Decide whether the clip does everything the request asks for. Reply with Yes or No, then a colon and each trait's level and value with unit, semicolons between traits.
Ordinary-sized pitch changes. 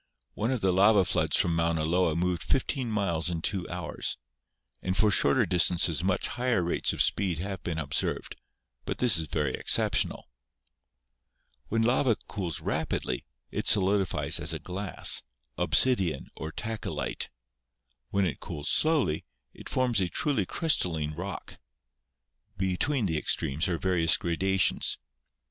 Yes: average, 4.1 semitones